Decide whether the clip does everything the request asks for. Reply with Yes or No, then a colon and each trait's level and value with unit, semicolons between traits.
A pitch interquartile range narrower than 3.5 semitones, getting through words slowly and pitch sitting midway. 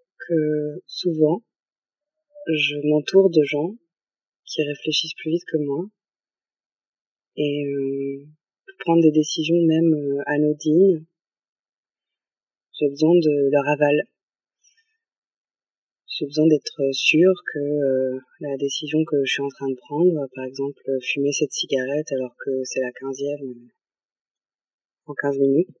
Yes: average, 2.8 semitones; slow, 125 wpm; medium, 150 Hz